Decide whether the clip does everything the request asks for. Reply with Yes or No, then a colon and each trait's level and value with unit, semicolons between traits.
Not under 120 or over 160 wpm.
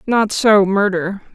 Yes: slow, 135 wpm